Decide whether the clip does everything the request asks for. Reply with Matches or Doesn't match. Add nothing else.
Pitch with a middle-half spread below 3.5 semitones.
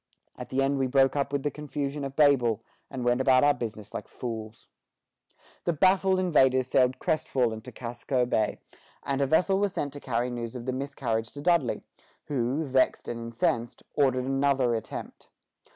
Matches